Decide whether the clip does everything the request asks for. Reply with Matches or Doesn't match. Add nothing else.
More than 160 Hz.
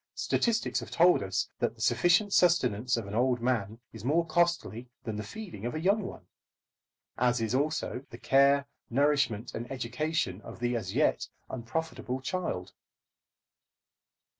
Doesn't match